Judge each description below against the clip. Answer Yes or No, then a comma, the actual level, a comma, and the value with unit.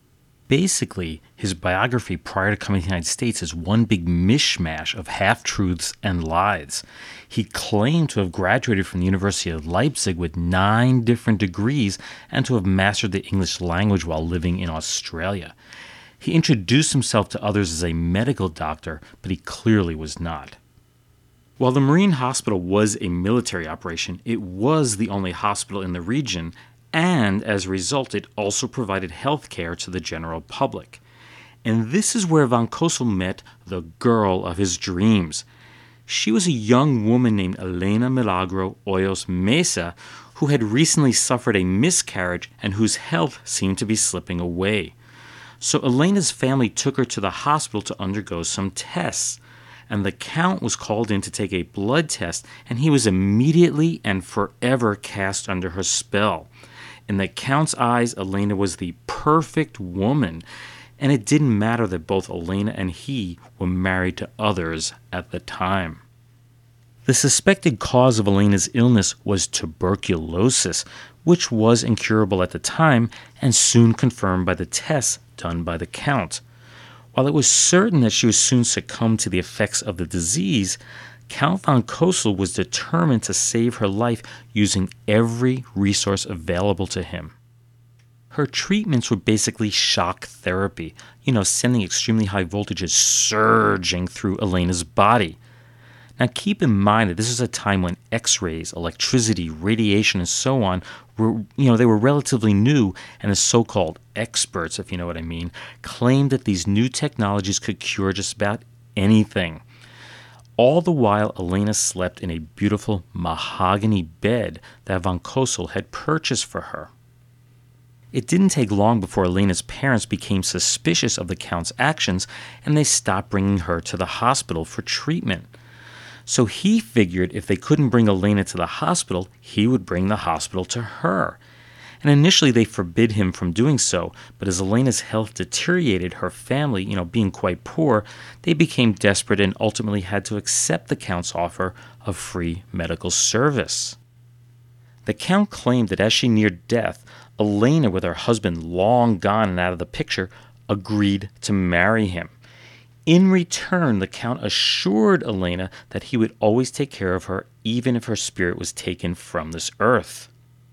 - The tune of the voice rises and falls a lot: No, average, 4.6 semitones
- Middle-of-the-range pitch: No, low, 110 Hz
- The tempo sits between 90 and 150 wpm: No, average, 160 wpm